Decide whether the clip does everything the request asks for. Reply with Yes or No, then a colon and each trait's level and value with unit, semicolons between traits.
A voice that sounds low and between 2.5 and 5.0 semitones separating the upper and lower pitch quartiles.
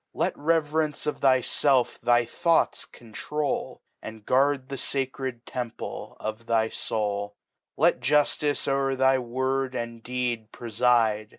Yes: low, 125 Hz; average, 3.0 semitones